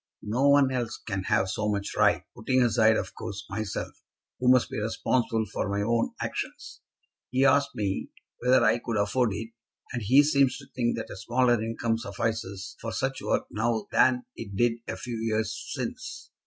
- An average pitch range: Yes, average, 3.0 semitones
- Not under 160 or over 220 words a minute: Yes, average, 180 wpm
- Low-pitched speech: Yes, low, 115 Hz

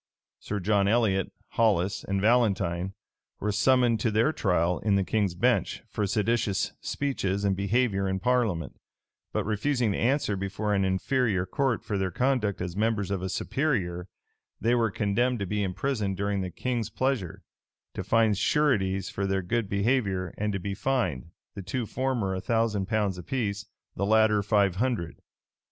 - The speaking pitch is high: No, low, 105 Hz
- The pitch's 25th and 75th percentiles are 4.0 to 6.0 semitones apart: No, average, 3.4 semitones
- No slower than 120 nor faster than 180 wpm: Yes, average, 165 wpm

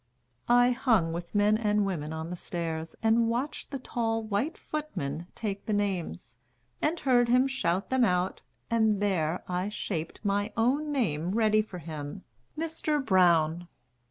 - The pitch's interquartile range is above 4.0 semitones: Yes, wide, 5.6 semitones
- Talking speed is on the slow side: No, average, 155 wpm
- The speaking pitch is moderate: No, high, 205 Hz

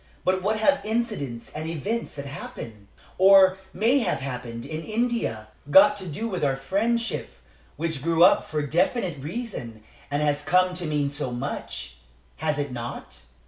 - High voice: No, medium, 160 Hz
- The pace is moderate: Yes, average, 160 wpm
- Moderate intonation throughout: No, wide, 6.6 semitones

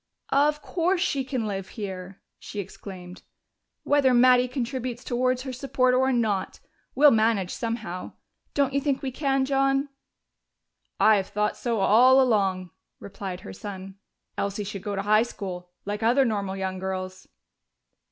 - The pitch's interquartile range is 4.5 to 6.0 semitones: Yes, average, 5.1 semitones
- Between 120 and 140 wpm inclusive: No, average, 150 wpm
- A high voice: Yes, high, 225 Hz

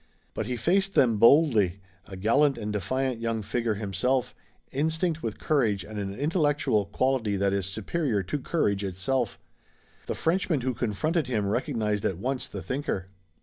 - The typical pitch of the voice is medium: No, low, 115 Hz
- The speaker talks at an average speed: Yes, average, 155 wpm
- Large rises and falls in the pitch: Yes, wide, 5.8 semitones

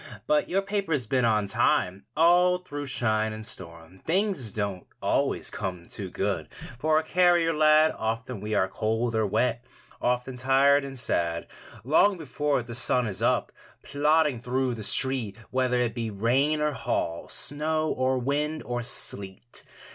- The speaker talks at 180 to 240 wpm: No, average, 155 wpm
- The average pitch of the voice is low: Yes, low, 125 Hz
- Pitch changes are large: Yes, wide, 5.8 semitones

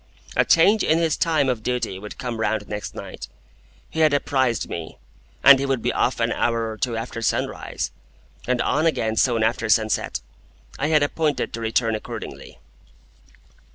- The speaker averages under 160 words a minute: No, average, 170 wpm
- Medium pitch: No, low, 120 Hz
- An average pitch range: Yes, average, 4.5 semitones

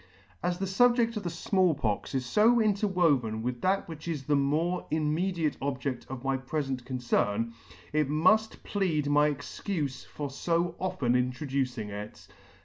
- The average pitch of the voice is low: No, medium, 150 Hz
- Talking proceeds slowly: No, average, 150 wpm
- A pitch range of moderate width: No, wide, 5.9 semitones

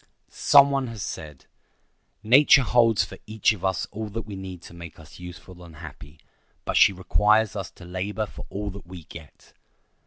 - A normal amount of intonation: Yes, average, 3.9 semitones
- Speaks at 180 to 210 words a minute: Yes, average, 185 wpm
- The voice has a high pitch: No, very low, 95 Hz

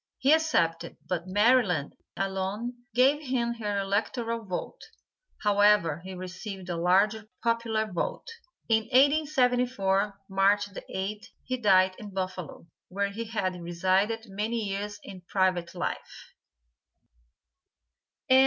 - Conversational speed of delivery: No, slow, 115 wpm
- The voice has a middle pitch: No, high, 205 Hz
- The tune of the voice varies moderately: Yes, average, 3.6 semitones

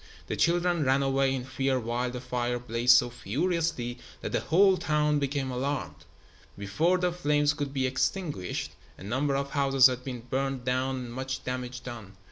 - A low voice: Yes, low, 130 Hz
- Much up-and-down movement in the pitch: No, average, 2.9 semitones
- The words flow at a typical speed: Yes, average, 175 wpm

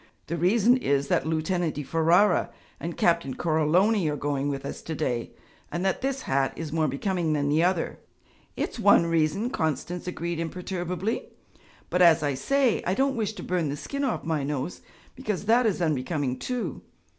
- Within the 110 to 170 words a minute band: No, average, 180 wpm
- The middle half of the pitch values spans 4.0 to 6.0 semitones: Yes, average, 4.6 semitones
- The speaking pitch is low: No, medium, 170 Hz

